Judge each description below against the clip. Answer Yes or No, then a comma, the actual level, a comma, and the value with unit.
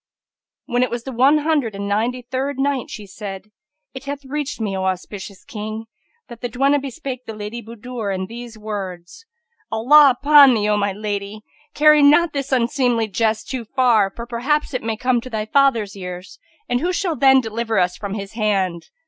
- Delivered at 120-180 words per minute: No, average, 190 wpm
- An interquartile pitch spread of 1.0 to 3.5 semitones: No, average, 4.4 semitones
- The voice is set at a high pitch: Yes, high, 235 Hz